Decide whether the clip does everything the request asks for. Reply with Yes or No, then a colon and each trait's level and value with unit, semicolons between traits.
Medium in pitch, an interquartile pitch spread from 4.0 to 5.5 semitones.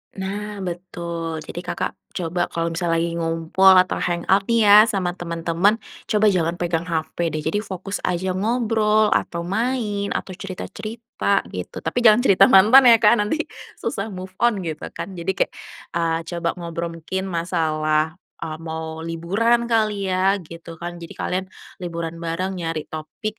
No: medium, 180 Hz; average, 3.6 semitones